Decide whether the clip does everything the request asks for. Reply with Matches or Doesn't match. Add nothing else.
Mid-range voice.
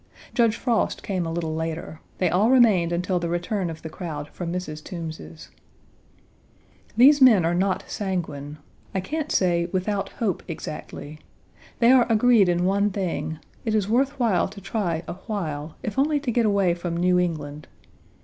Matches